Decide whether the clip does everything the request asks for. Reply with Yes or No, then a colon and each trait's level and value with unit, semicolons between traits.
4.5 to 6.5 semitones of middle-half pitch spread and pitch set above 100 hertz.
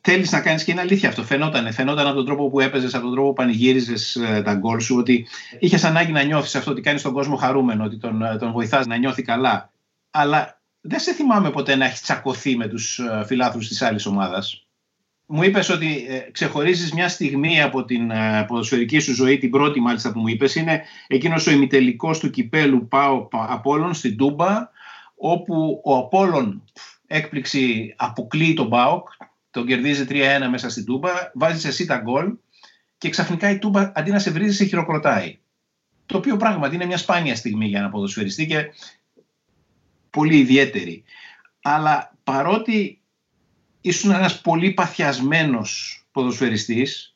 Yes: average, 5.2 semitones; medium, 140 Hz